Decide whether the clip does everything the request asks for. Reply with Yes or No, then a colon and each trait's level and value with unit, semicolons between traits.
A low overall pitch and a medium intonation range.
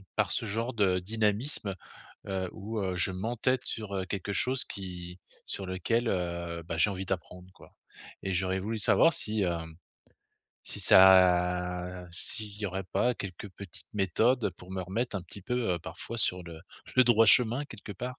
Yes: very low, 95 Hz; average, 3.7 semitones